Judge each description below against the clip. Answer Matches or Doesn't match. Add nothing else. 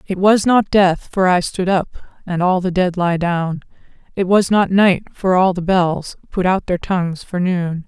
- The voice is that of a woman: Matches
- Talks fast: Matches